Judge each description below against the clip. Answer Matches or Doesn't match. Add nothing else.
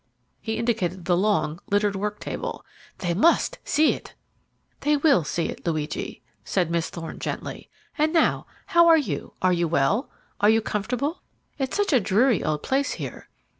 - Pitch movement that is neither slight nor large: Doesn't match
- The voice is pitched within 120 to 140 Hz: Doesn't match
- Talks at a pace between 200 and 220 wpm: Doesn't match